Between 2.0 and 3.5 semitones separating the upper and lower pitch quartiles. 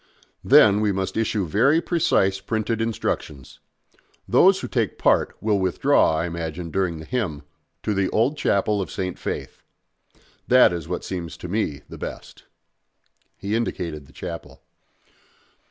No: average, 4.4 semitones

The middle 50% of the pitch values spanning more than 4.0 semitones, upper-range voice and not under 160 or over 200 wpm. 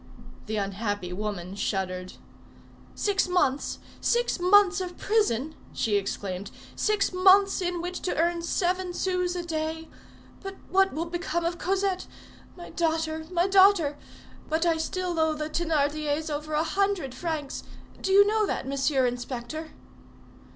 No: average, 4.7 semitones; very high, 330 Hz; average, 140 wpm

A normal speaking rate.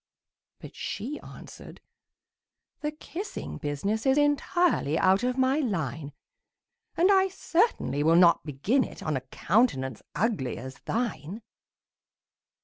No: slow, 120 wpm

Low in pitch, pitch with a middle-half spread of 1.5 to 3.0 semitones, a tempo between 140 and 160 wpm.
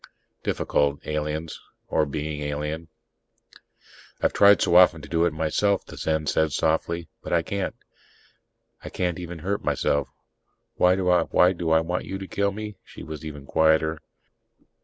Yes: very low, 80 Hz; average, 2.7 semitones; average, 150 wpm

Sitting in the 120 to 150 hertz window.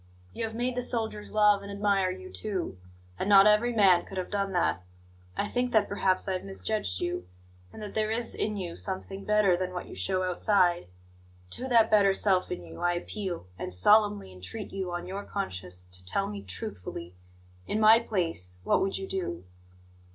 No: high, 195 Hz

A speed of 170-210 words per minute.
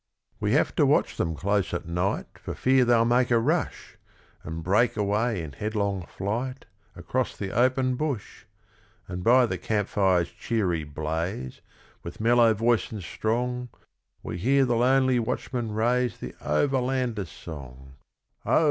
No: average, 150 wpm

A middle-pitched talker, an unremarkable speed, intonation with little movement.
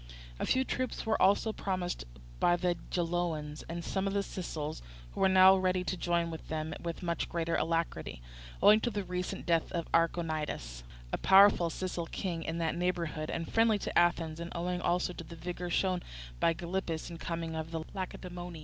Yes: medium, 175 Hz; average, 180 wpm; narrow, 2.1 semitones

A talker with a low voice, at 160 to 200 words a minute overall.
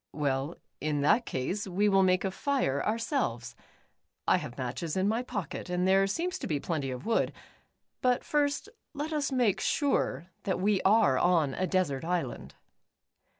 No: medium, 185 Hz; average, 170 wpm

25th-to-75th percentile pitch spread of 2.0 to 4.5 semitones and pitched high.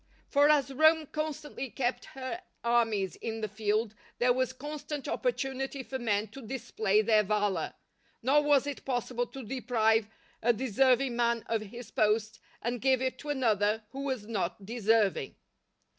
Yes: average, 3.7 semitones; high, 240 Hz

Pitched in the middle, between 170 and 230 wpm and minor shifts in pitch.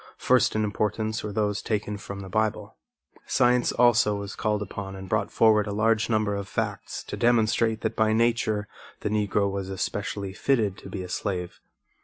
No: low, 105 Hz; average, 180 wpm; narrow, 1.6 semitones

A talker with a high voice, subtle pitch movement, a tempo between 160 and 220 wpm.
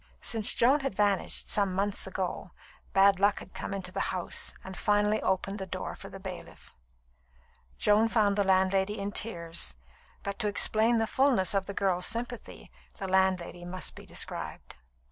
Yes: high, 195 Hz; narrow, 1.9 semitones; average, 165 wpm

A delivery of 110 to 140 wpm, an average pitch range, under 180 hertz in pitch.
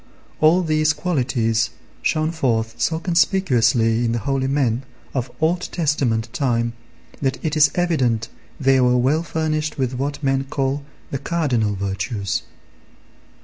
Yes: slow, 135 wpm; average, 4.8 semitones; low, 135 Hz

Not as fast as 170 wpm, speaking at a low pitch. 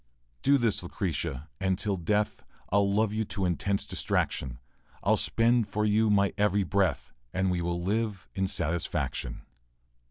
Yes: average, 150 wpm; low, 100 Hz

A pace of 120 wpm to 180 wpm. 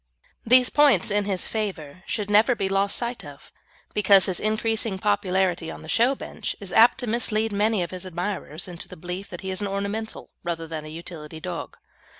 No: average, 195 wpm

